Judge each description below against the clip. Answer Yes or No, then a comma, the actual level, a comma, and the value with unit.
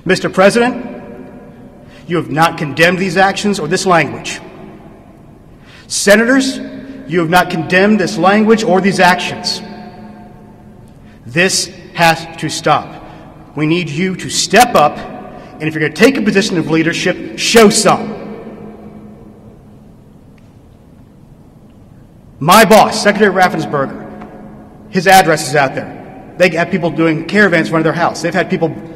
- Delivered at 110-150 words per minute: Yes, slow, 135 wpm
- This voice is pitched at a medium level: Yes, medium, 180 Hz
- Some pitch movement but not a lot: Yes, average, 3.1 semitones